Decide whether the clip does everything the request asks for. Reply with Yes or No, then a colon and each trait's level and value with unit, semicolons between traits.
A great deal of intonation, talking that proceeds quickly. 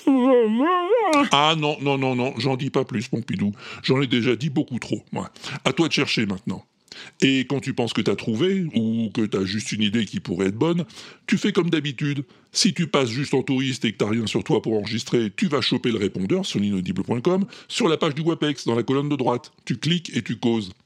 Yes: wide, 6.4 semitones; fast, 225 wpm